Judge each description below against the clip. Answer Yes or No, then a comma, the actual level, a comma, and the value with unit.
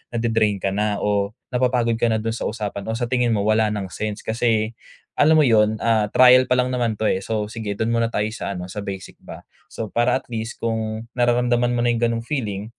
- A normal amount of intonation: No, narrow, 2.2 semitones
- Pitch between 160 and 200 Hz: No, low, 115 Hz